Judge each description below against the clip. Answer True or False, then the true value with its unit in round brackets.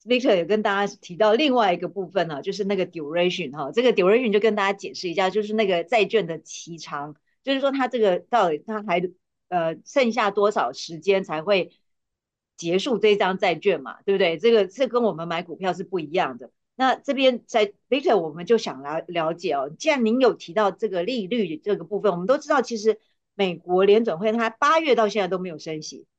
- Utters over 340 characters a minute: True (360 characters per minute)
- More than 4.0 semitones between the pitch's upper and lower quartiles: True (4.5 semitones)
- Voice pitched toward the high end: True (205 Hz)